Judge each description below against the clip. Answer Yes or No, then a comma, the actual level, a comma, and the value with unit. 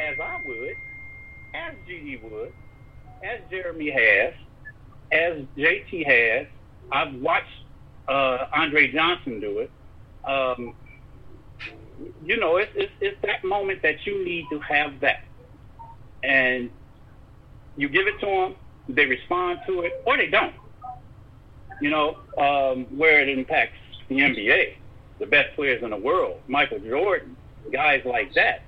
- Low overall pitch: No, medium, 150 Hz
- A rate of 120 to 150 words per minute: Yes, slow, 135 wpm